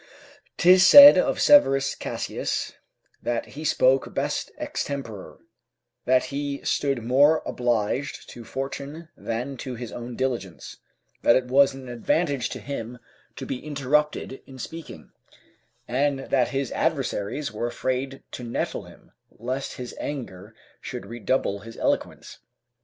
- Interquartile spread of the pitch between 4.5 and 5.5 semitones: No, average, 2.9 semitones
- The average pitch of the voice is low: Yes, low, 130 Hz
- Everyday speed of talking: No, slow, 130 wpm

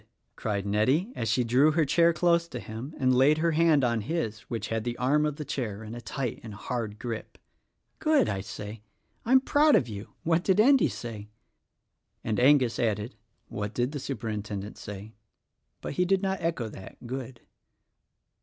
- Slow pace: No, average, 180 wpm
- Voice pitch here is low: Yes, low, 125 Hz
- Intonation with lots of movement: Yes, wide, 6.5 semitones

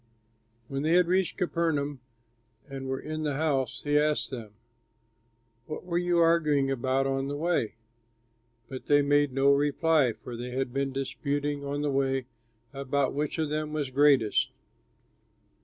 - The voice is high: No, medium, 140 Hz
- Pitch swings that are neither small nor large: No, narrow, 2.3 semitones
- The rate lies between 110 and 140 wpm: No, average, 155 wpm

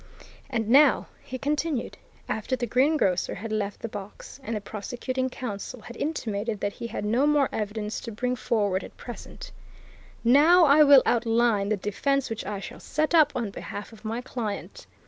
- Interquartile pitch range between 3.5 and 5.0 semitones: Yes, average, 4.2 semitones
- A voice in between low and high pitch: No, high, 235 Hz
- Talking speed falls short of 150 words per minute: No, average, 175 wpm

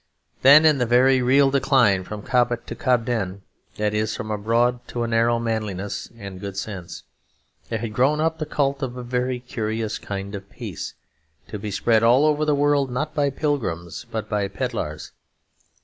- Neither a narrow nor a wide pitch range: Yes, average, 4.1 semitones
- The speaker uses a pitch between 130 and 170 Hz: No, low, 120 Hz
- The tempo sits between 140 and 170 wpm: No, average, 180 wpm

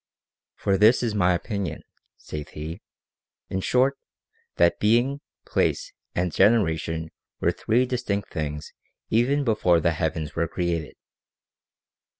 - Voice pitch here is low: Yes, very low, 95 Hz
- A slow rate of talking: Yes, slow, 130 wpm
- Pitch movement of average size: No, wide, 6.2 semitones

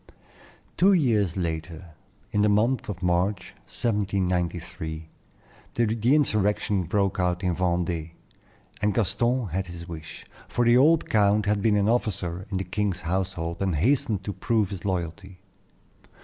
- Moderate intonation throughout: Yes, average, 3.3 semitones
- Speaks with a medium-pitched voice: No, very low, 95 Hz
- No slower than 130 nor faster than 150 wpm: Yes, average, 140 wpm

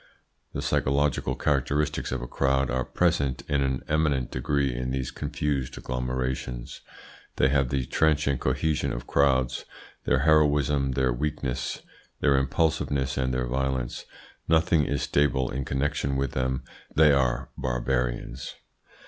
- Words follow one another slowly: Yes, slow, 130 wpm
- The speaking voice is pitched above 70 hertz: No, very low, 65 Hz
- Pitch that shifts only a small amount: Yes, narrow, 2.2 semitones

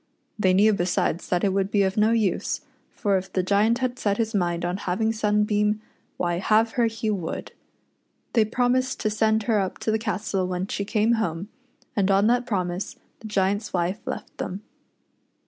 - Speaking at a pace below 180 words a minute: No, average, 185 wpm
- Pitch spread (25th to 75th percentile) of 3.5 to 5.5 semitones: No, average, 2.7 semitones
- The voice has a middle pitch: No, high, 205 Hz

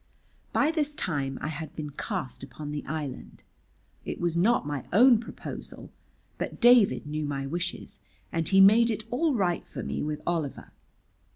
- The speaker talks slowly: No, average, 165 wpm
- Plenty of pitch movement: Yes, wide, 7.2 semitones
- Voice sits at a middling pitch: Yes, medium, 170 Hz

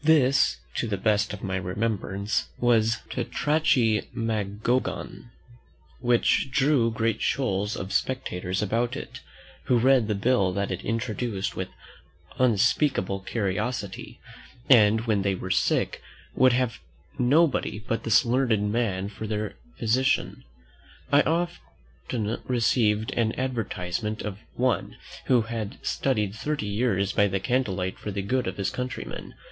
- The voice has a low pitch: Yes, low, 110 Hz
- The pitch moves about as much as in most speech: Yes, average, 3.9 semitones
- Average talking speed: No, slow, 130 wpm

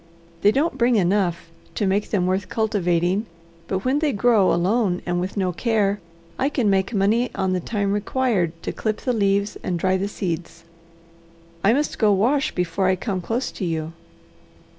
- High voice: Yes, high, 200 Hz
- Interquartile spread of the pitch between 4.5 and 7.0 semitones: No, average, 3.6 semitones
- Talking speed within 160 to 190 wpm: Yes, average, 180 wpm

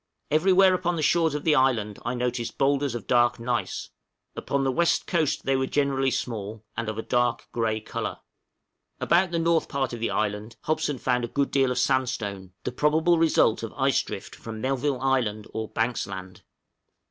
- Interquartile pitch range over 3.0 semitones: Yes, average, 4.5 semitones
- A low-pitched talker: Yes, low, 130 Hz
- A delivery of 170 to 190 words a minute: Yes, average, 185 wpm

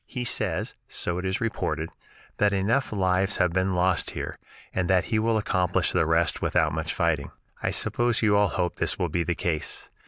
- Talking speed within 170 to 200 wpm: Yes, average, 195 wpm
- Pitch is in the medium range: No, very low, 95 Hz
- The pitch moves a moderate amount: Yes, average, 3.3 semitones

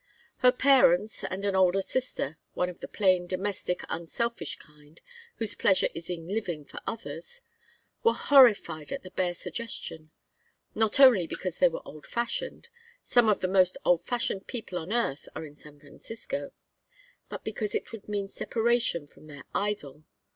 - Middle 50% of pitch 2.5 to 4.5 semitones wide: No, average, 5.3 semitones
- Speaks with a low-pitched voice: No, high, 190 Hz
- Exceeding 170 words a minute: No, average, 160 wpm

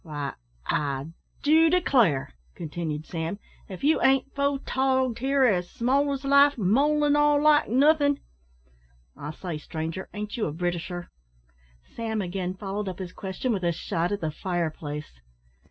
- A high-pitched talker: Yes, high, 205 Hz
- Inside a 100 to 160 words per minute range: Yes, average, 155 wpm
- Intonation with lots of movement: Yes, wide, 8.5 semitones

